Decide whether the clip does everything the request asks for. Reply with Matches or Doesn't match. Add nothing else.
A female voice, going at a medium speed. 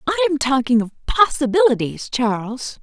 Doesn't match